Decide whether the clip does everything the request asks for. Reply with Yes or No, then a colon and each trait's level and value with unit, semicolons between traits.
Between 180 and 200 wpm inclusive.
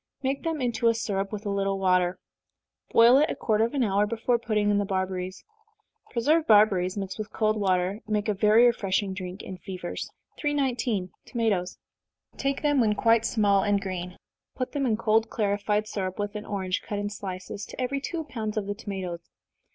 Yes: average, 190 wpm